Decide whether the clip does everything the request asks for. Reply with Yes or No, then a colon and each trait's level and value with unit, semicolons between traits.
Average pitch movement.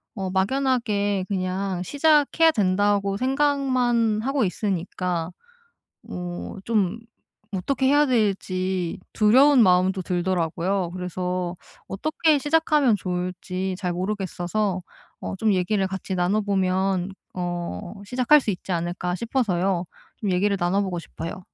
Yes: average, 3.9 semitones